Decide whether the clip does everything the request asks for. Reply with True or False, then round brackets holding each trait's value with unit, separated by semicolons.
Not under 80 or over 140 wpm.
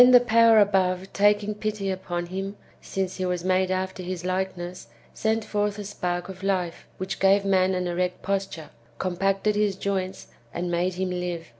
False (170 wpm)